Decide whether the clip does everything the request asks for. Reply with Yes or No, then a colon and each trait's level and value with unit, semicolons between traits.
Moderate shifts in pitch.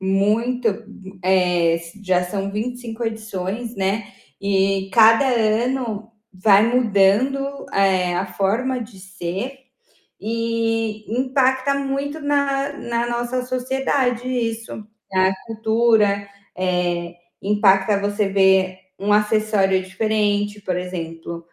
Yes: average, 3.9 semitones